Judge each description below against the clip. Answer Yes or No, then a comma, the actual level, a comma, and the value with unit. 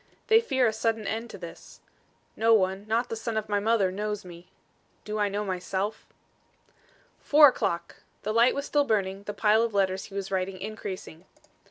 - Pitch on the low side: No, high, 210 Hz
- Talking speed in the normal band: Yes, average, 185 wpm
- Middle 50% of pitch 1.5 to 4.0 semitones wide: Yes, average, 3.0 semitones